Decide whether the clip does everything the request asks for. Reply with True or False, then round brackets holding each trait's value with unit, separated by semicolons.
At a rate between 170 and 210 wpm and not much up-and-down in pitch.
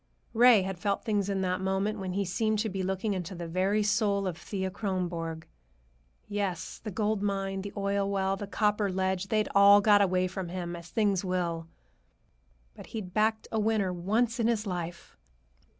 True (180 wpm; 2.3 semitones)